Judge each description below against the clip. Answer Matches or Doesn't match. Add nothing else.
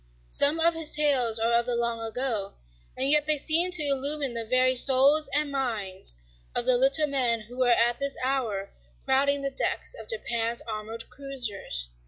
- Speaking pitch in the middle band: Doesn't match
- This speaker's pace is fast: Doesn't match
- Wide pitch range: Doesn't match